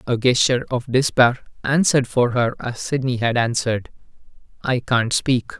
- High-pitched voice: No, low, 125 Hz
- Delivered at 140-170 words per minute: Yes, average, 150 wpm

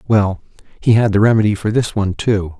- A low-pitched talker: Yes, low, 105 Hz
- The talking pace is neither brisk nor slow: No, fast, 210 wpm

